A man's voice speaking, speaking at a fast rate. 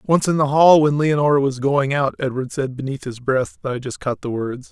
Yes: male; fast, 240 wpm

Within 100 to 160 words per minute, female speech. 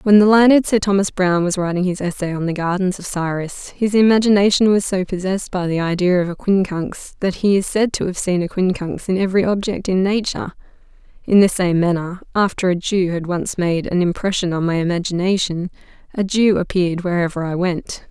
No: average, 200 wpm; female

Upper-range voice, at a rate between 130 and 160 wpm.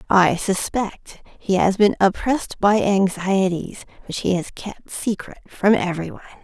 Yes: high, 195 Hz; average, 150 wpm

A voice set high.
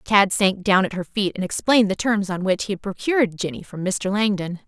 Yes: high, 195 Hz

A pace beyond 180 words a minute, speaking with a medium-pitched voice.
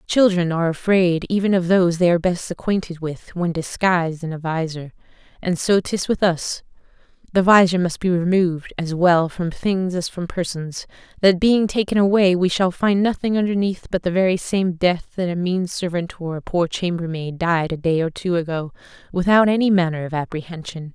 Yes: average, 190 wpm; medium, 175 Hz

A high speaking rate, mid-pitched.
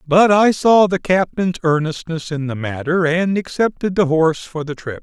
No: average, 190 wpm; medium, 170 Hz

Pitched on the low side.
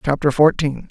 No: medium, 145 Hz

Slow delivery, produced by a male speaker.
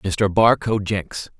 Yes: slow, 130 wpm; male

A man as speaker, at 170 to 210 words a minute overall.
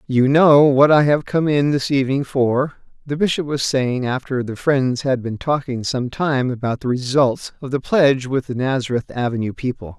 Yes: male; average, 200 wpm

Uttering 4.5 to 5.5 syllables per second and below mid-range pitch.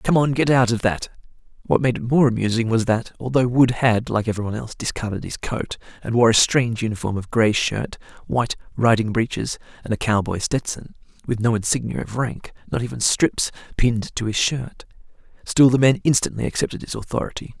No: 5.7 syllables/s; low, 115 Hz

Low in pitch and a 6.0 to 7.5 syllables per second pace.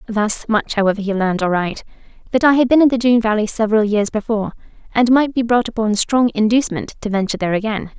No: high, 220 Hz; 6.8 syllables/s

